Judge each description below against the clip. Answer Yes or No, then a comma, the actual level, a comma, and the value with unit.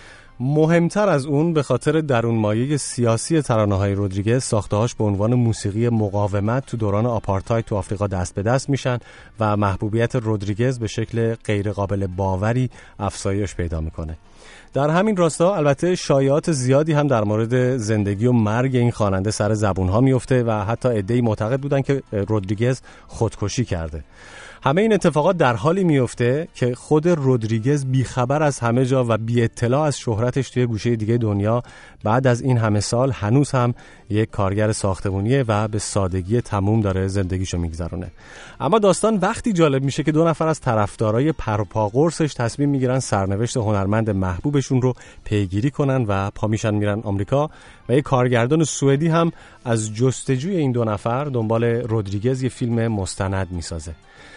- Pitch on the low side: Yes, low, 115 Hz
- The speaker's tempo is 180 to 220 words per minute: No, average, 155 wpm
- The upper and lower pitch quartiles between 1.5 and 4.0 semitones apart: No, average, 4.5 semitones